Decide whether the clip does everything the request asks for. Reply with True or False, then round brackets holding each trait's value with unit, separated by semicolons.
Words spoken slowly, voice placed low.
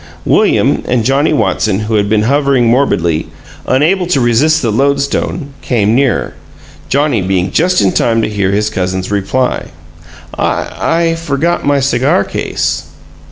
False (145 wpm; 125 Hz)